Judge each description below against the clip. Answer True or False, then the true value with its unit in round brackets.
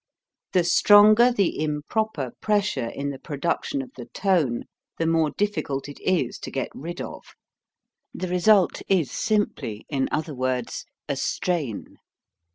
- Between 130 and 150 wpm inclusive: True (140 wpm)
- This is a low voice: False (165 Hz)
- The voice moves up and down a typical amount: False (6.8 semitones)